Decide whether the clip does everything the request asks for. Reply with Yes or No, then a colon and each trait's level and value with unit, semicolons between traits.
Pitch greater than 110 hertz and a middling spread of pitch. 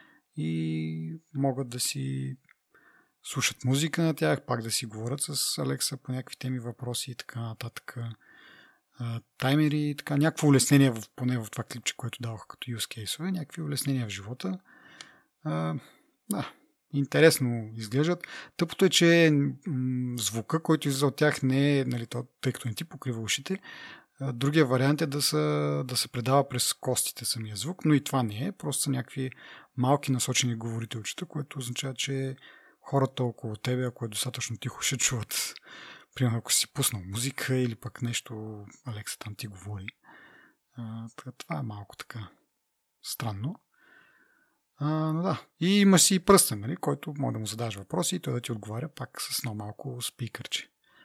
Yes: low, 130 Hz; average, 4.1 semitones